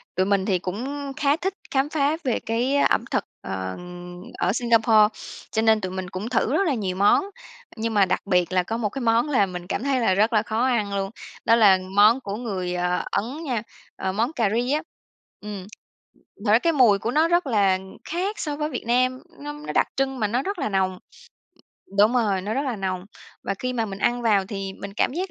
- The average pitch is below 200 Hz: No, high, 225 Hz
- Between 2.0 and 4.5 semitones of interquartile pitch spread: No, average, 5.2 semitones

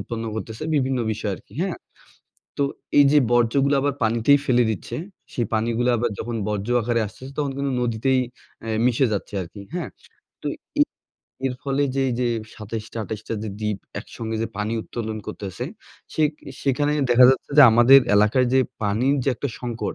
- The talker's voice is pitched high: No, low, 120 Hz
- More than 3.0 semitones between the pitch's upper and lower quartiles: Yes, average, 3.4 semitones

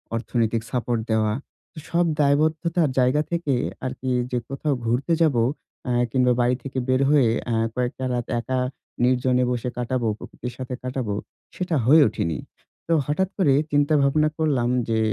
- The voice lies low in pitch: Yes, low, 130 Hz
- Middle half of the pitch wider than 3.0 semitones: Yes, average, 3.4 semitones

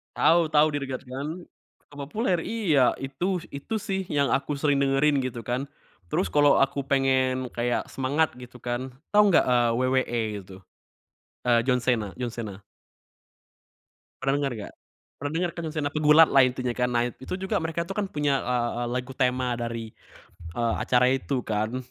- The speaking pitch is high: No, low, 130 Hz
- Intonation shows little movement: No, average, 3.3 semitones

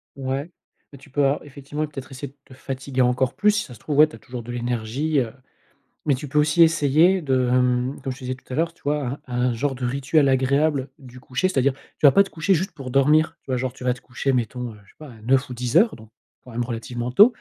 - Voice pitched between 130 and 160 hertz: Yes, low, 135 Hz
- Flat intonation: No, average, 3.0 semitones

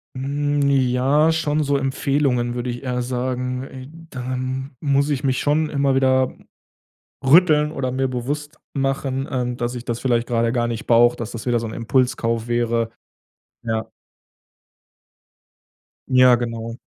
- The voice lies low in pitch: Yes, low, 130 Hz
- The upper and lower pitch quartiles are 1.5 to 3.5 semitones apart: Yes, narrow, 2.5 semitones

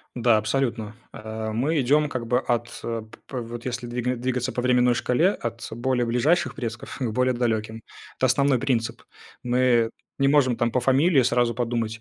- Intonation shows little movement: Yes, narrow, 1.8 semitones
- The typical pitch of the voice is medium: No, low, 120 Hz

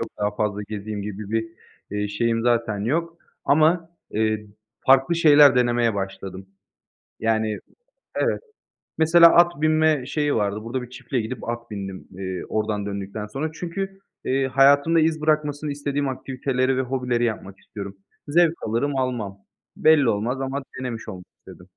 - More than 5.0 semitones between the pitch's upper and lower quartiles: Yes, wide, 5.4 semitones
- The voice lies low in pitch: Yes, low, 125 Hz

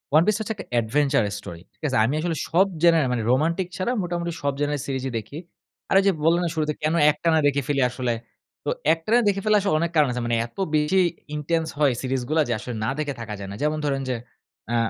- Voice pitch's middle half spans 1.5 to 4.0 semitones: No, average, 4.5 semitones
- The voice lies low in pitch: No, medium, 150 Hz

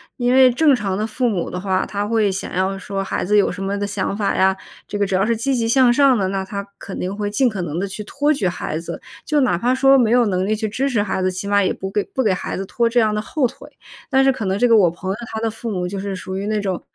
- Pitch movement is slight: No, average, 3.8 semitones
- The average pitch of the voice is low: No, high, 205 Hz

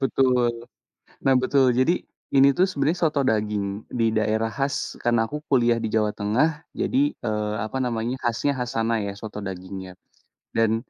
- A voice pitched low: Yes, low, 115 Hz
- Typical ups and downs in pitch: Yes, average, 3.8 semitones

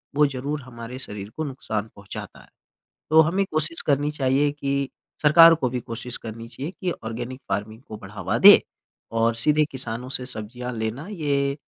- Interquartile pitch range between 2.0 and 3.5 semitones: No, average, 4.4 semitones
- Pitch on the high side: No, low, 130 Hz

